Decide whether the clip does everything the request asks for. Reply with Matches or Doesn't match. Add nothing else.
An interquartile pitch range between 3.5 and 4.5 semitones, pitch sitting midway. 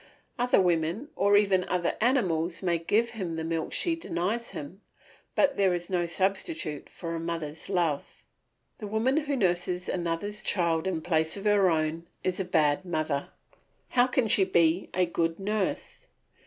Matches